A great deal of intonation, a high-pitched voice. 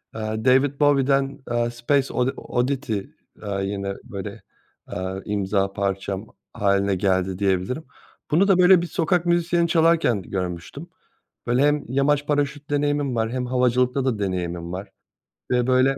No: wide, 6.6 semitones; low, 125 Hz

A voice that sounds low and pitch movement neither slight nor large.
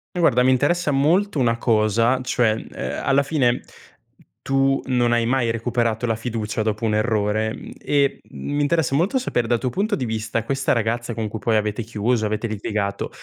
Yes: low, 120 Hz; average, 3.6 semitones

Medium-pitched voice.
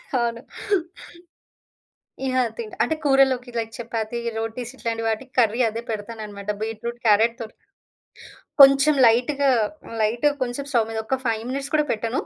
No: high, 235 Hz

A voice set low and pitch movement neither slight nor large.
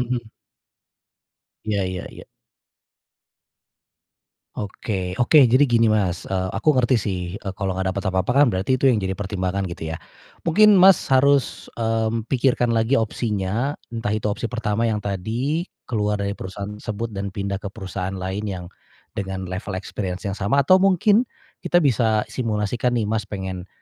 Yes: low, 105 Hz; average, 4.1 semitones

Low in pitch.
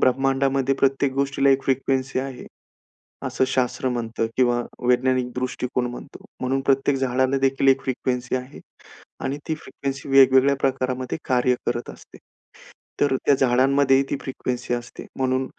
Yes: low, 130 Hz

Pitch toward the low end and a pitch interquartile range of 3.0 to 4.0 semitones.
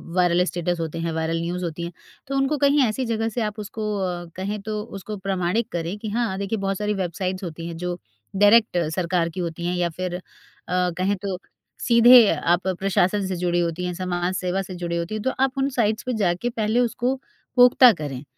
No: medium, 185 Hz; average, 3.7 semitones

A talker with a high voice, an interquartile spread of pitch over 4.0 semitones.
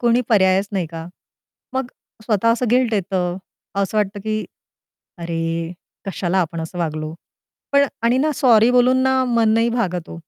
Yes: high, 205 Hz; wide, 5.5 semitones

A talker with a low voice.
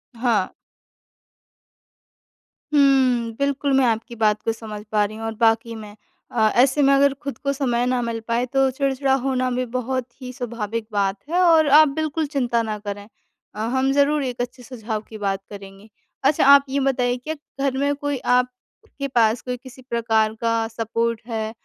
No: high, 245 Hz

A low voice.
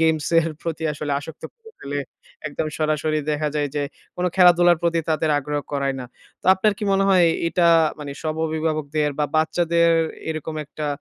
No: medium, 155 Hz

